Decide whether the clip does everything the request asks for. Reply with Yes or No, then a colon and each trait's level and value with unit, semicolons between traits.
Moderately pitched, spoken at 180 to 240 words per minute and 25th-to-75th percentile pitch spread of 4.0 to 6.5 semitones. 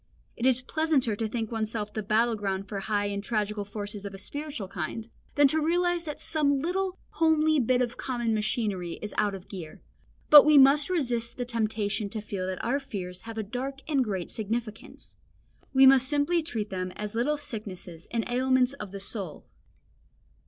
No: high, 230 Hz; average, 185 wpm; average, 5.2 semitones